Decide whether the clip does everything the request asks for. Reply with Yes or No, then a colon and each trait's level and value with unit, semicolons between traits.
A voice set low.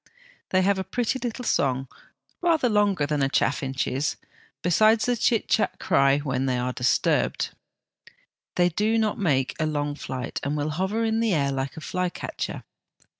No: medium, 160 Hz